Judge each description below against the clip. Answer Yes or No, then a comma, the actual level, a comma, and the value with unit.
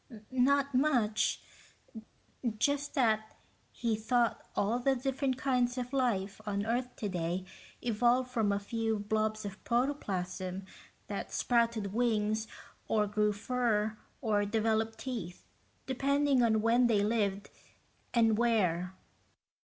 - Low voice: No, high, 225 Hz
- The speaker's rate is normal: No, slow, 115 wpm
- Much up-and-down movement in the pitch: No, average, 3.1 semitones